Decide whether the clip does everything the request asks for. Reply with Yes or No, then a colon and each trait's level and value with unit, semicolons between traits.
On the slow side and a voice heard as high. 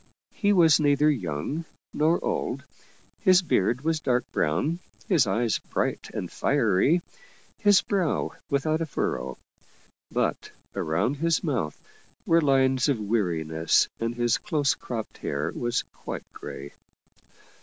No: slow, 125 wpm; medium, 140 Hz